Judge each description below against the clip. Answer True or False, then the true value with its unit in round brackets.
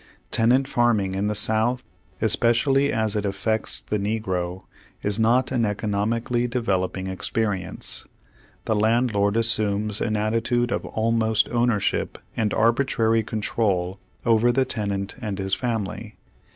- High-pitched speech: False (110 Hz)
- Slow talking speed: True (130 wpm)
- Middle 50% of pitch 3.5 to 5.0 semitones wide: False (2.5 semitones)